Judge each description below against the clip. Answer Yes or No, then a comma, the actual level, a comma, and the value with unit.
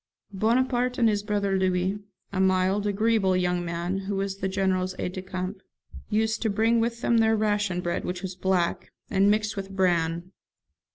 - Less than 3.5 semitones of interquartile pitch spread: Yes, narrow, 2.6 semitones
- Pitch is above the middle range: Yes, high, 195 Hz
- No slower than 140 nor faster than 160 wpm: No, average, 175 wpm